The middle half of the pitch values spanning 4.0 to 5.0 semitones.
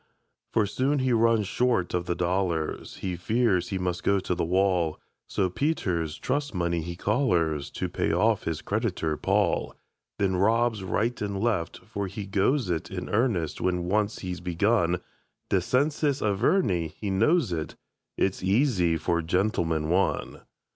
Yes: average, 4.6 semitones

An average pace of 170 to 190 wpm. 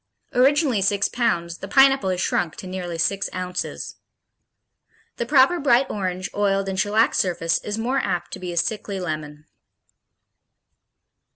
No: average, 145 wpm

